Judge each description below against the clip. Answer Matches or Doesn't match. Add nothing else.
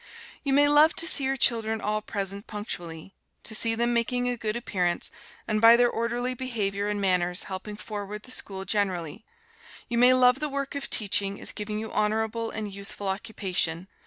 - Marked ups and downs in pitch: Doesn't match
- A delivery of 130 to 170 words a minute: Doesn't match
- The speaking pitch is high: Matches